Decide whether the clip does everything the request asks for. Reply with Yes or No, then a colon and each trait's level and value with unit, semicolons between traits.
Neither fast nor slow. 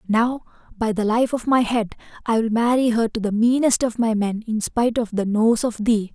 No: fast, 235 wpm